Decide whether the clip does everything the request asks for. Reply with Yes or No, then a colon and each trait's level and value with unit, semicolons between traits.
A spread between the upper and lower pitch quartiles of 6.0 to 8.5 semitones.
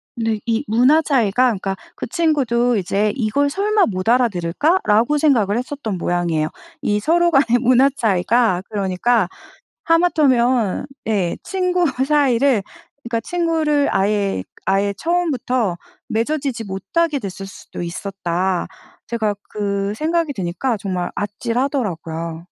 Yes: wide, 6.4 semitones